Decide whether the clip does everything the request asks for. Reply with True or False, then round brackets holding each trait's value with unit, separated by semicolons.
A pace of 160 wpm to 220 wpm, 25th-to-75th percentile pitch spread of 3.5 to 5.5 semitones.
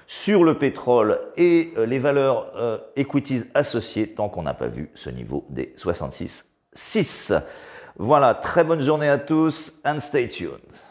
False (150 wpm; 4.8 semitones)